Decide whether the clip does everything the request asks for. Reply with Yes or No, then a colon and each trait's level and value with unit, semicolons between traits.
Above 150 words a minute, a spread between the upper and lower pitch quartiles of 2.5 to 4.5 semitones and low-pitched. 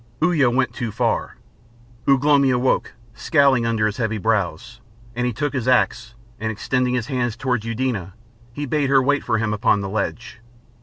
Yes: average, 175 wpm; average, 3.1 semitones; low, 120 Hz